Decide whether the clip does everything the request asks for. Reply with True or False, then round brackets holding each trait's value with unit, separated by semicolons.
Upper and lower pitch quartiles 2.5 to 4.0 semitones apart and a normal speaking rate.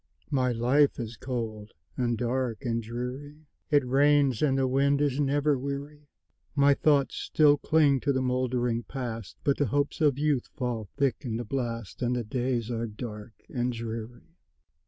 True (3.2 semitones; 165 wpm)